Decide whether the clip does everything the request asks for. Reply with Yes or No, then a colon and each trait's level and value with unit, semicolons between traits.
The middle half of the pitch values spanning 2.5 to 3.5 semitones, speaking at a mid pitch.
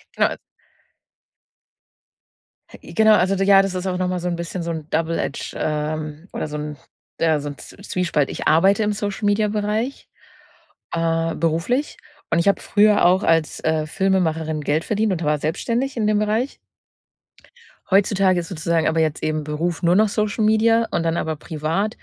No: average, 4.6 semitones; medium, 175 Hz